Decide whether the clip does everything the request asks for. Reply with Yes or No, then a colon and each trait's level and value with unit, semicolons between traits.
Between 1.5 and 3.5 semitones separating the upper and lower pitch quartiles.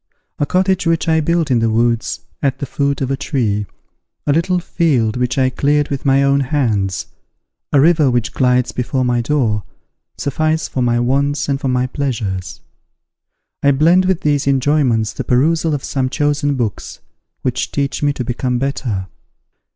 Yes: average, 3.2 semitones